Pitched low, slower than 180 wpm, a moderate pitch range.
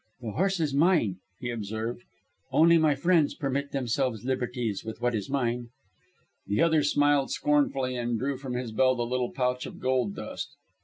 Yes: low, 130 Hz; average, 170 wpm; average, 3.3 semitones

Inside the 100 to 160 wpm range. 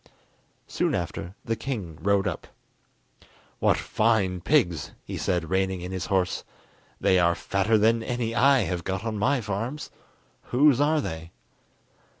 Yes: average, 145 wpm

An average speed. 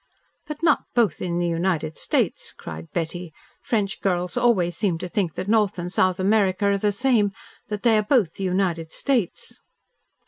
Yes: average, 175 wpm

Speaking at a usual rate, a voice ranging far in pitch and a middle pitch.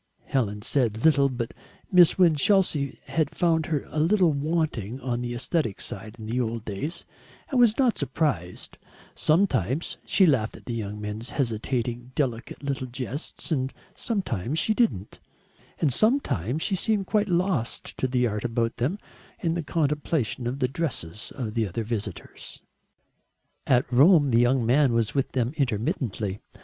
No: average, 155 wpm; wide, 5.7 semitones; low, 130 Hz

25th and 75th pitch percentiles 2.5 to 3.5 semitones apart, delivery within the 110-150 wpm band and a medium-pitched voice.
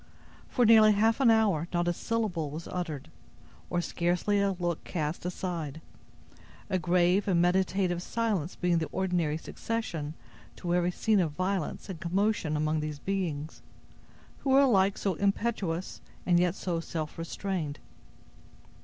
Yes: average, 3.2 semitones; average, 145 wpm; medium, 180 Hz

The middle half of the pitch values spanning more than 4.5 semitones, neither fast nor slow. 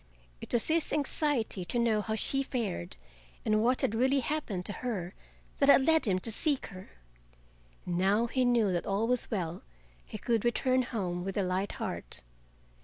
Yes: average, 5.0 semitones; average, 180 wpm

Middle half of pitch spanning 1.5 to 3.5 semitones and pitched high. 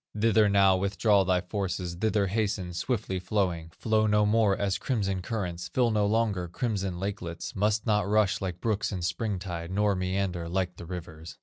No: average, 2.8 semitones; low, 100 Hz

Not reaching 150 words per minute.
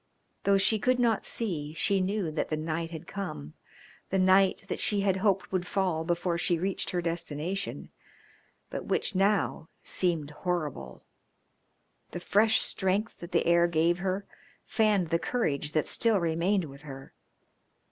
No: average, 155 wpm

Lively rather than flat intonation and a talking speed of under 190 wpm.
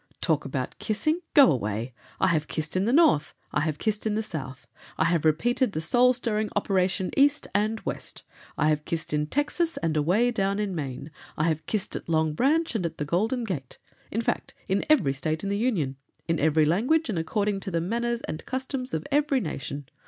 No: wide, 7.4 semitones; fast, 205 wpm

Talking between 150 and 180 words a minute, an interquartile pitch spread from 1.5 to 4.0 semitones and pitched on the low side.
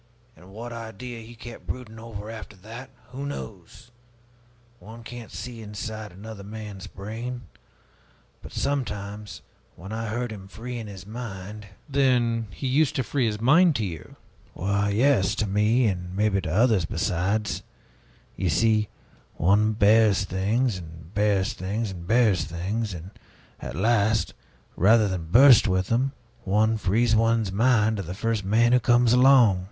Yes: average, 155 wpm; average, 3.2 semitones; low, 110 Hz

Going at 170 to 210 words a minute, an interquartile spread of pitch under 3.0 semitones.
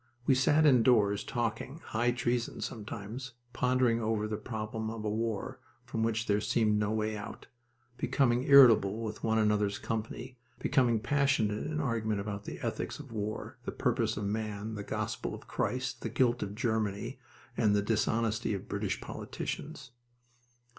No: average, 155 wpm; narrow, 2.6 semitones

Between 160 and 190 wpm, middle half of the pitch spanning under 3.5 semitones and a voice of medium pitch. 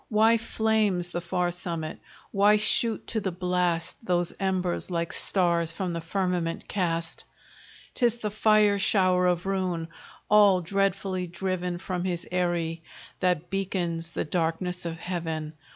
No: slow, 135 wpm; narrow, 2.4 semitones; medium, 180 Hz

